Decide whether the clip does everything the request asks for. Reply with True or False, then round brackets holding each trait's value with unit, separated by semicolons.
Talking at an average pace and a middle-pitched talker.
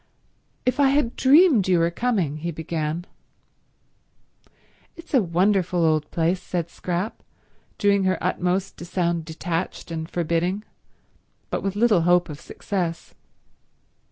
False (130 wpm; 180 Hz)